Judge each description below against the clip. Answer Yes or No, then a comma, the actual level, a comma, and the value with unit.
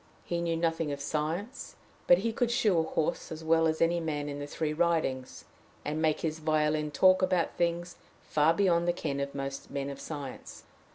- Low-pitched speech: No, medium, 160 Hz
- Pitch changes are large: No, narrow, 2.4 semitones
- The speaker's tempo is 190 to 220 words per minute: Yes, average, 195 wpm